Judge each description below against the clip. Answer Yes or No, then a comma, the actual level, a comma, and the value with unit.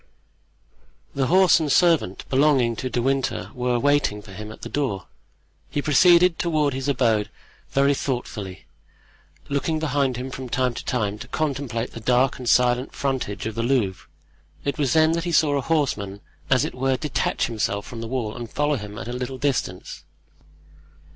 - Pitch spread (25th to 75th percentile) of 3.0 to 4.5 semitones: Yes, average, 3.8 semitones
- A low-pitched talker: Yes, low, 130 Hz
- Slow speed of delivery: No, average, 175 wpm